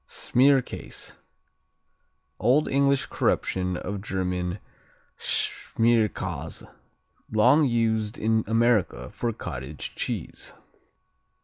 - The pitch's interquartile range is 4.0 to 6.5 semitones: Yes, average, 4.3 semitones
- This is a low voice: Yes, low, 110 Hz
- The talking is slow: Yes, slow, 75 wpm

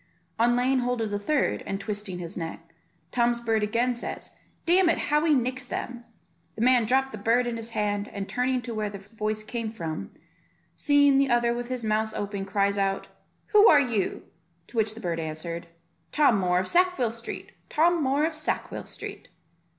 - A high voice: Yes, high, 230 Hz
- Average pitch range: Yes, average, 3.9 semitones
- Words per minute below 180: No, average, 190 wpm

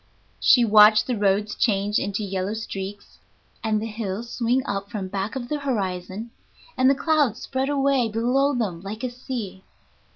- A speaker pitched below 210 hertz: No, high, 220 Hz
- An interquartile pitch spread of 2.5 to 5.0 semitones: Yes, average, 4.1 semitones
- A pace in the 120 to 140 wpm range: No, average, 165 wpm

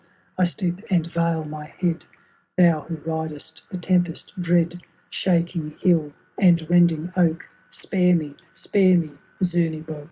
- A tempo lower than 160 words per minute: Yes, slow, 135 wpm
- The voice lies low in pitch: No, medium, 170 Hz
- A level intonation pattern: Yes, narrow, 1.9 semitones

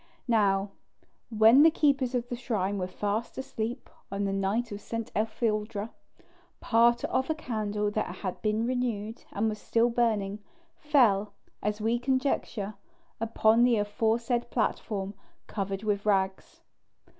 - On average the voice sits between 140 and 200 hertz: No, high, 220 Hz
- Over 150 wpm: No, slow, 135 wpm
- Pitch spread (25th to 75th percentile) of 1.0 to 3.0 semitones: Yes, average, 2.7 semitones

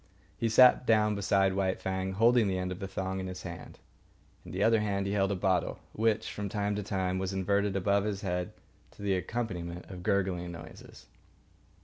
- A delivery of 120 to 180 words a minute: No, average, 200 wpm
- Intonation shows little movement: Yes, narrow, 1.9 semitones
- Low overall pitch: Yes, very low, 95 Hz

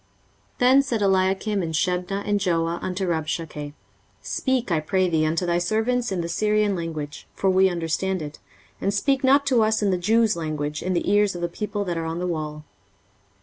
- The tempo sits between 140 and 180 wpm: No, average, 200 wpm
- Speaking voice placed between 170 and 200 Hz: Yes, medium, 185 Hz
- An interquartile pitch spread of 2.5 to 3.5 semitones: No, average, 4.0 semitones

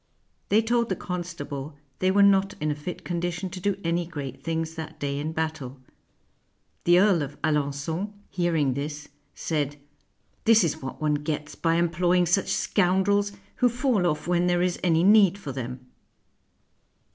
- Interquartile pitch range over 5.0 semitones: No, average, 3.9 semitones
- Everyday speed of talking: Yes, average, 160 wpm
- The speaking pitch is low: No, medium, 170 Hz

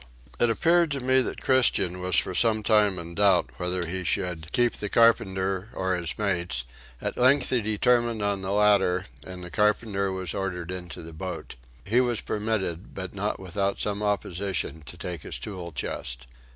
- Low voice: Yes, very low, 95 Hz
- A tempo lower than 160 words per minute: No, average, 175 wpm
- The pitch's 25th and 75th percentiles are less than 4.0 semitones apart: Yes, average, 3.3 semitones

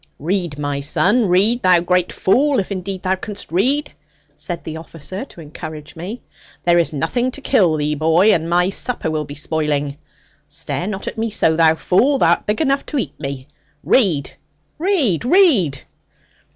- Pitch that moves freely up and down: Yes, wide, 5.8 semitones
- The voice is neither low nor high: Yes, medium, 175 Hz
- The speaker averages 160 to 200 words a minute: Yes, average, 175 wpm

